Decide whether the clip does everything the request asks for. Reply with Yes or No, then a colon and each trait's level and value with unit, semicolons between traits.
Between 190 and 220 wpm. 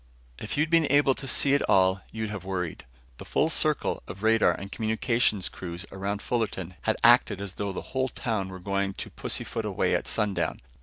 Yes: average, 195 wpm